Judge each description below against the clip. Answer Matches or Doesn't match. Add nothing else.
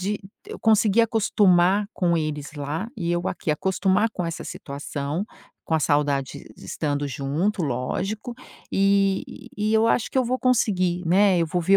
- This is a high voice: Doesn't match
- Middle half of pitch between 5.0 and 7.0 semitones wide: Matches